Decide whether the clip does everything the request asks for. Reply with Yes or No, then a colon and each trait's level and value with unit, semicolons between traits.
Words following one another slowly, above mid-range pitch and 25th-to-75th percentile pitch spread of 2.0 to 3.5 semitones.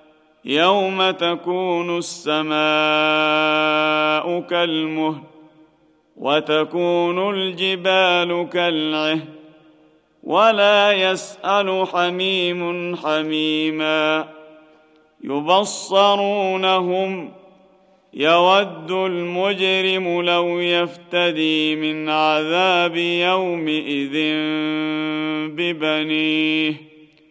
No: slow, 45 wpm; medium, 170 Hz; average, 3.0 semitones